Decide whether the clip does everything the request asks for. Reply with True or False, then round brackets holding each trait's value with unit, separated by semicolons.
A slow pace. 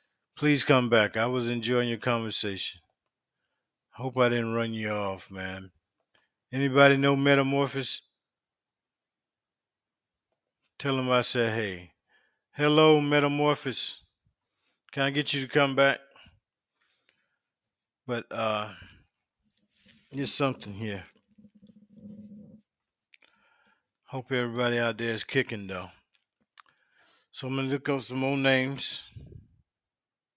True (105 wpm)